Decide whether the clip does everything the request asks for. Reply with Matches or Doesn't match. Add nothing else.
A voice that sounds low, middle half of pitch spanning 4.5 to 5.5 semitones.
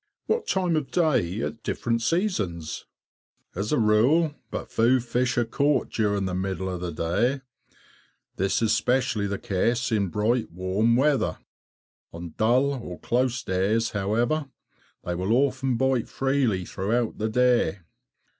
Matches